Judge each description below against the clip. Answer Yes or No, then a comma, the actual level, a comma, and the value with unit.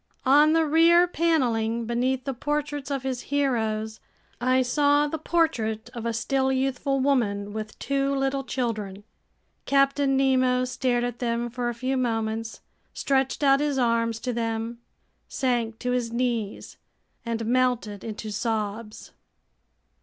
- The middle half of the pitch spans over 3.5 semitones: No, average, 3.1 semitones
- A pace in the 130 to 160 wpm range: Yes, average, 140 wpm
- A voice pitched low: No, very high, 250 Hz